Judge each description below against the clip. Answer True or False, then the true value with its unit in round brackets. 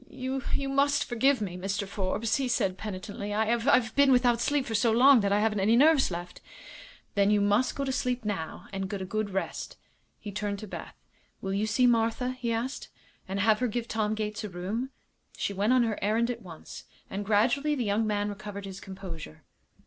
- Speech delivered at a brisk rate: True (210 wpm)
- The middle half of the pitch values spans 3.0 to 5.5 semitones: True (3.6 semitones)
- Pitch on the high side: True (215 Hz)